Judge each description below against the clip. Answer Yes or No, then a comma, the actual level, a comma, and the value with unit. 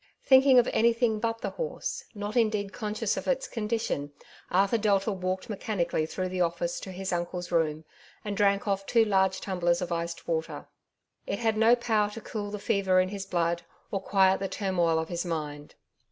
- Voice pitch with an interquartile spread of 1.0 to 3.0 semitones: No, average, 3.7 semitones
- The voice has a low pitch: No, high, 195 Hz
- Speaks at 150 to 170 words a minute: No, average, 185 wpm